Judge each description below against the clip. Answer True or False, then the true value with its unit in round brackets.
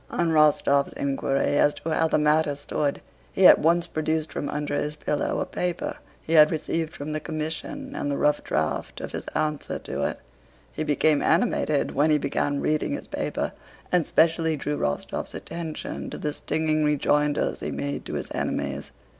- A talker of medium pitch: True (150 Hz)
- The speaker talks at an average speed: True (180 wpm)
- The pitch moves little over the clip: True (1.8 semitones)